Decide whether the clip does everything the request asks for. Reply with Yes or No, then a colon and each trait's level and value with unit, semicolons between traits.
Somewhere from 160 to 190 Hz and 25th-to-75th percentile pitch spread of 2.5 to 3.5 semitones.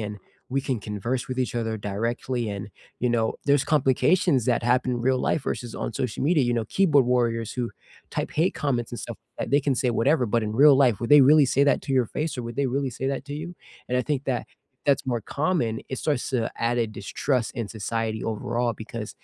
No: low, 125 Hz; average, 3.2 semitones